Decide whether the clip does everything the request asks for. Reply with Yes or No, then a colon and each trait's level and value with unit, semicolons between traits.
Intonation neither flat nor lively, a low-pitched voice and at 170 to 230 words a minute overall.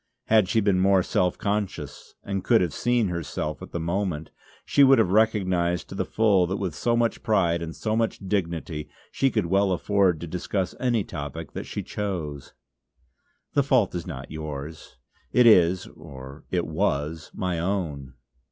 Yes: average, 4.3 semitones; very low, 90 Hz; average, 175 wpm